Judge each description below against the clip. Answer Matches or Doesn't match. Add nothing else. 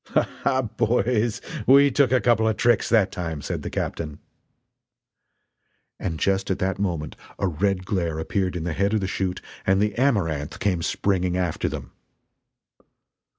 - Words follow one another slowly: Doesn't match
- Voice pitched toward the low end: Matches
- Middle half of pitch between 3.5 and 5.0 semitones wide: Matches